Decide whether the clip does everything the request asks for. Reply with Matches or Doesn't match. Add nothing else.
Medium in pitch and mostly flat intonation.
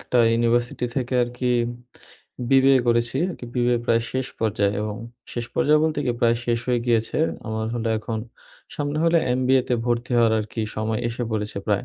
Doesn't match